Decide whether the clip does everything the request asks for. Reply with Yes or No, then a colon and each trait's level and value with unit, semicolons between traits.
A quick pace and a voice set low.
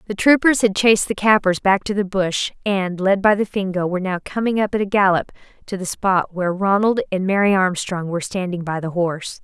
No: fast, 225 wpm; high, 195 Hz